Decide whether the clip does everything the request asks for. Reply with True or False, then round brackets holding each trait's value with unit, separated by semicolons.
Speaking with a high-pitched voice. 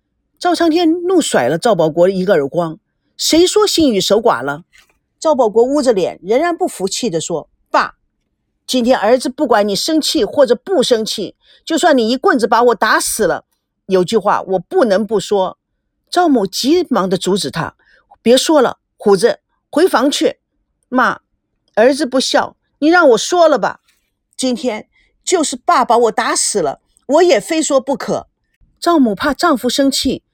True (260 Hz)